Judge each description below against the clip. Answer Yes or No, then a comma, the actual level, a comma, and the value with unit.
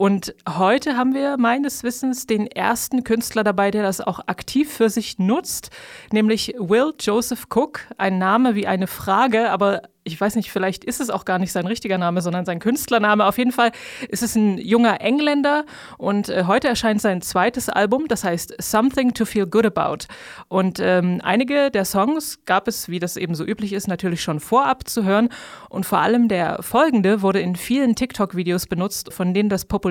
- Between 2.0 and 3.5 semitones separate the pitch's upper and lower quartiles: No, average, 4.4 semitones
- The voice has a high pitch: Yes, high, 215 Hz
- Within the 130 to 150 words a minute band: No, fast, 190 wpm